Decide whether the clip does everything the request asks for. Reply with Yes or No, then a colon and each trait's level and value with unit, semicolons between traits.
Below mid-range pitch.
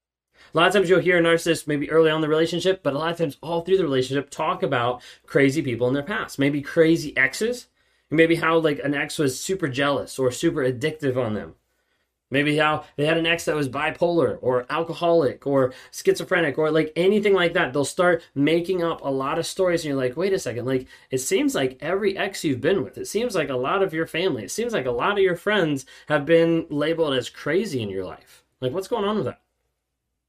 No: medium, 155 Hz